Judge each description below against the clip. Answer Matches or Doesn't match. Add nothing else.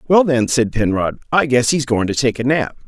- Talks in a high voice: Doesn't match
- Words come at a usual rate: Doesn't match